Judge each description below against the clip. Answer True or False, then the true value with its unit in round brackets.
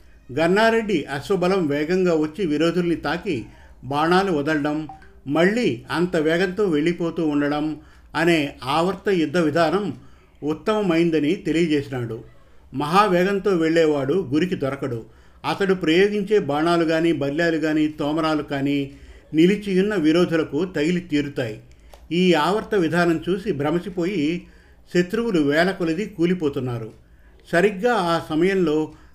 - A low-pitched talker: False (165 Hz)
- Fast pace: False (95 wpm)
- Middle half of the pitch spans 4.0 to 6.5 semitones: False (3.4 semitones)